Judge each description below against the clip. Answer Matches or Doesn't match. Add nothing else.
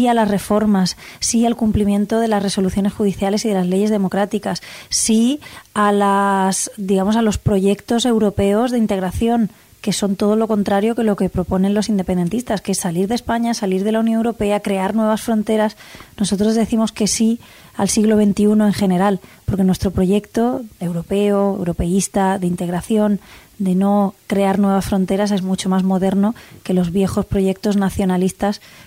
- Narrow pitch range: Matches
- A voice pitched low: Doesn't match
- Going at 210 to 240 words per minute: Doesn't match